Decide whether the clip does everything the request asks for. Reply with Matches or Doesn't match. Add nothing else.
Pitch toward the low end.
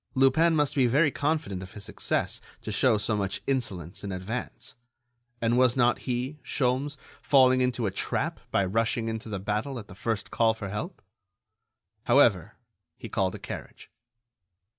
Matches